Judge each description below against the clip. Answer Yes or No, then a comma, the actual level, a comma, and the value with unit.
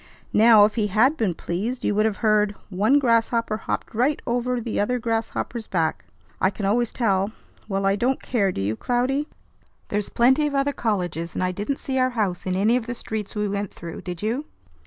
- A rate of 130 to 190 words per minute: No, fast, 205 wpm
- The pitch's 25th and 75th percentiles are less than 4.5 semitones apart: Yes, average, 3.6 semitones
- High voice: Yes, high, 220 Hz